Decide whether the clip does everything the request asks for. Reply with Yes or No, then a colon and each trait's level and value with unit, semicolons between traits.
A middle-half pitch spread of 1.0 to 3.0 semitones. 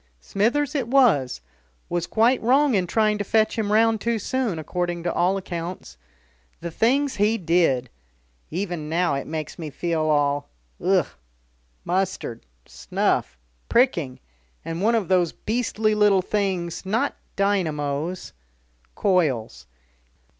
No: average, 5.3 semitones